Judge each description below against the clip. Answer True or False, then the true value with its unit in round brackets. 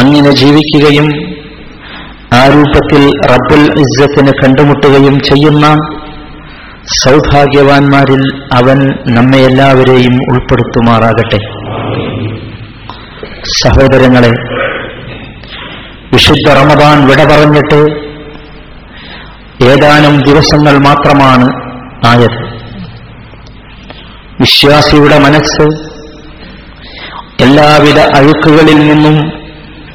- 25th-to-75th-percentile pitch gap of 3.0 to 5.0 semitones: False (2.6 semitones)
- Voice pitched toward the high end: False (140 Hz)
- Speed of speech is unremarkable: False (55 wpm)